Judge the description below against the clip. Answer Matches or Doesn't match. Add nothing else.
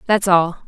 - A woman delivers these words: Matches